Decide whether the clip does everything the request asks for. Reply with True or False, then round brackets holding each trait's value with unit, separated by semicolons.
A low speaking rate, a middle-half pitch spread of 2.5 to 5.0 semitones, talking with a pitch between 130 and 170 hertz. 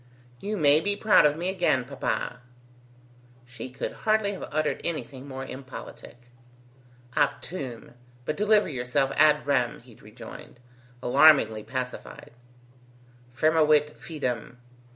True (110 wpm; 4.1 semitones; 140 Hz)